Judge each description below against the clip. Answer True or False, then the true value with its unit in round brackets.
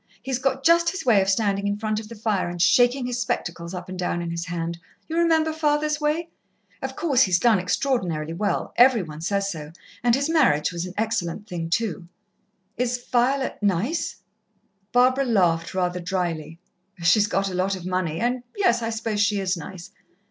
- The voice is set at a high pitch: True (205 Hz)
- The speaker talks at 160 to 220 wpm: True (190 wpm)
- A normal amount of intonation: False (6.0 semitones)